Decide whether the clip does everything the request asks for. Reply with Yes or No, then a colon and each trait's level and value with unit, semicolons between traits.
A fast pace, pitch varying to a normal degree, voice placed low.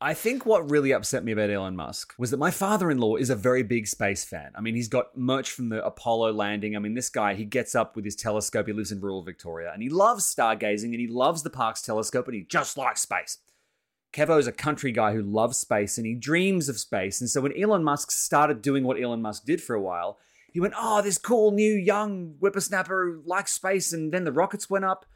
No: fast, 250 wpm; wide, 8.5 semitones; low, 125 Hz